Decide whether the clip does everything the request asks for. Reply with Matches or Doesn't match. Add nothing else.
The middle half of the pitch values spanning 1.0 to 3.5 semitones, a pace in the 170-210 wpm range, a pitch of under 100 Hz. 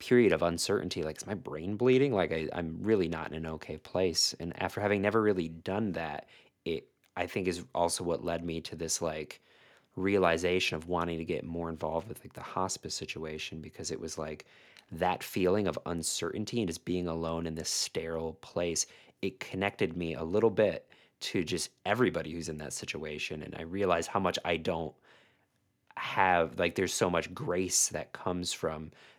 Matches